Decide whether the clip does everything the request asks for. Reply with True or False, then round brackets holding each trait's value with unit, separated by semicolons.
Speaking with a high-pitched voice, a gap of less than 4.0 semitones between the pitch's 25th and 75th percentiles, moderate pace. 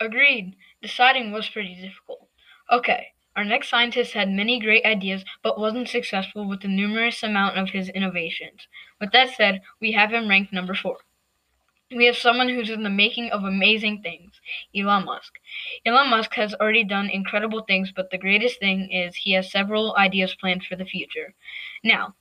True (210 Hz; 3.2 semitones; 175 wpm)